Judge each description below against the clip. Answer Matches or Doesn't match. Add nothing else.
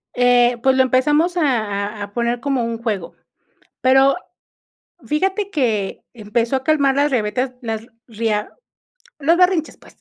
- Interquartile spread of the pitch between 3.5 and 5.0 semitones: Matches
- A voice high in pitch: Matches